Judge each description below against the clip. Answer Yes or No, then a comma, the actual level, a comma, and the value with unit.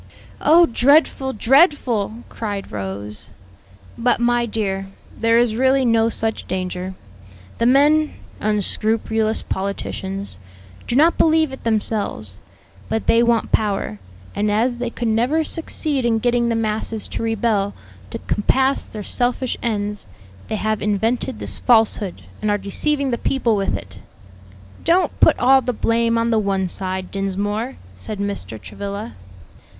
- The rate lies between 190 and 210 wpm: No, average, 140 wpm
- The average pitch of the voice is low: No, high, 225 Hz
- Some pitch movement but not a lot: Yes, average, 3.3 semitones